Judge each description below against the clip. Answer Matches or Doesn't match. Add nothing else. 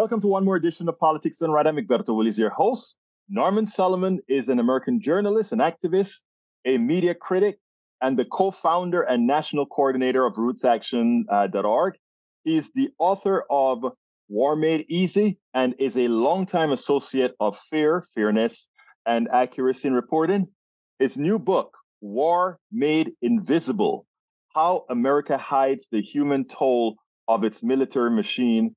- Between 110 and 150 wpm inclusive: Matches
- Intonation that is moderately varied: Doesn't match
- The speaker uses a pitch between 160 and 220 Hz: Doesn't match